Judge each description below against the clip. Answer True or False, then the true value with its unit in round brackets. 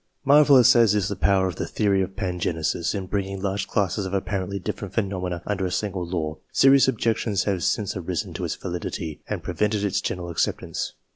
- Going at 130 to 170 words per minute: False (190 wpm)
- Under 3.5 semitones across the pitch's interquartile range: True (2.5 semitones)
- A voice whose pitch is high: False (95 Hz)